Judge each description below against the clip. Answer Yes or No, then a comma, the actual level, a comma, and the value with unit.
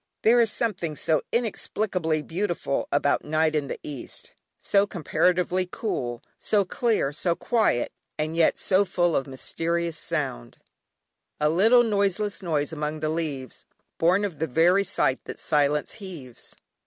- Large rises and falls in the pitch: No, average, 4.8 semitones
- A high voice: No, medium, 170 Hz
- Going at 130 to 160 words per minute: Yes, average, 140 wpm